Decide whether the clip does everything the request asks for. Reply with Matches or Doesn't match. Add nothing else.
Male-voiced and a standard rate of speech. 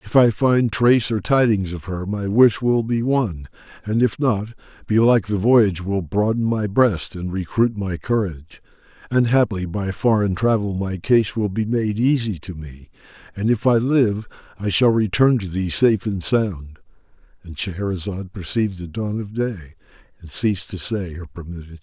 Matches